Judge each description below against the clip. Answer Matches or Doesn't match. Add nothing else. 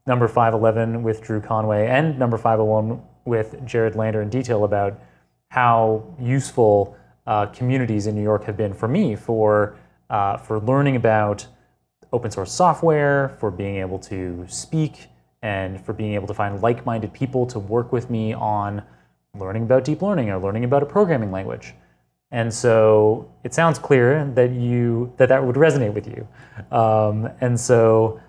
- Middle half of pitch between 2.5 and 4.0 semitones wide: Matches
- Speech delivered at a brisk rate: Doesn't match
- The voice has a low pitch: Matches